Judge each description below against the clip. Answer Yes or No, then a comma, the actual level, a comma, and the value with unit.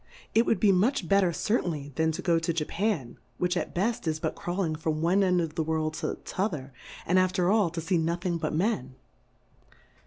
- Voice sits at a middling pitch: Yes, medium, 170 Hz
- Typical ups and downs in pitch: Yes, average, 3.2 semitones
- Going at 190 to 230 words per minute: Yes, fast, 205 wpm